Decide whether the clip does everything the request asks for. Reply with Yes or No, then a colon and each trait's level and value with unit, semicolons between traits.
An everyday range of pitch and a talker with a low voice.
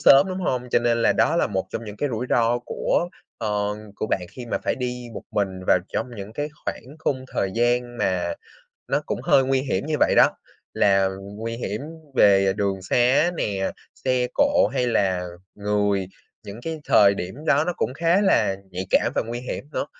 Yes: average, 4.7 semitones; low, 115 Hz